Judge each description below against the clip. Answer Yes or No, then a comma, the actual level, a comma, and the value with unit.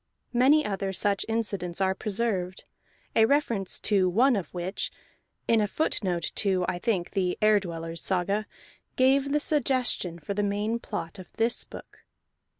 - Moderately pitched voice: No, high, 205 Hz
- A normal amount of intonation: Yes, average, 4.1 semitones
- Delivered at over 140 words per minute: Yes, average, 150 wpm